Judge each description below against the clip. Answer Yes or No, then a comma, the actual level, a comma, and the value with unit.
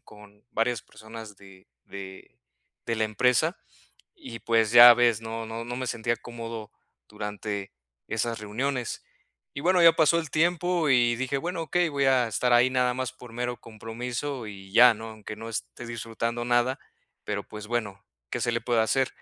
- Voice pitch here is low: Yes, low, 120 Hz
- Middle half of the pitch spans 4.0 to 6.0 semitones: No, average, 2.7 semitones